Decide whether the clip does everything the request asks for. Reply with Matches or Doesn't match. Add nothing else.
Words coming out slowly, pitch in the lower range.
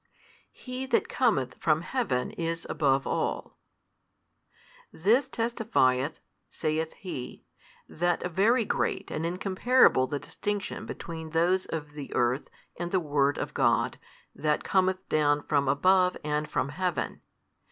Doesn't match